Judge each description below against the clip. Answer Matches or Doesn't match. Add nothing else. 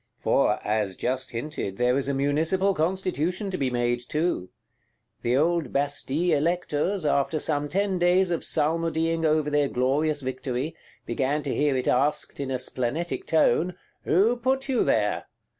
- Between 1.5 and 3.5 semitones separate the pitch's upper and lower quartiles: Doesn't match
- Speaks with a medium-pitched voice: Matches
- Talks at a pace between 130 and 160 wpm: Matches